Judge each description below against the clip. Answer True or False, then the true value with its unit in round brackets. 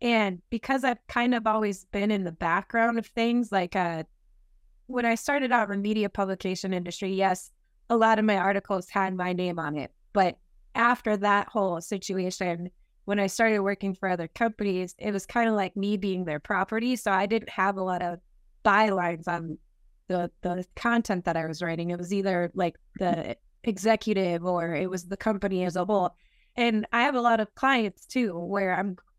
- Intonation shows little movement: False (3.6 semitones)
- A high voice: True (195 Hz)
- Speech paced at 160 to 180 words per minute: False (195 wpm)